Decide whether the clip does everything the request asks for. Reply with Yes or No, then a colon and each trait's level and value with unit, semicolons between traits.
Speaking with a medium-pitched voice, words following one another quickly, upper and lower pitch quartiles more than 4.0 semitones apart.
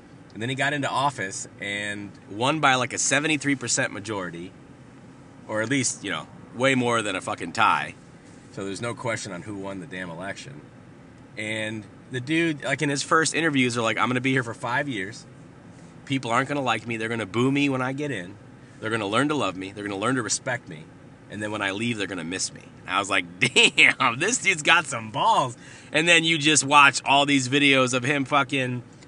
No: low, 130 Hz; fast, 220 wpm; average, 4.7 semitones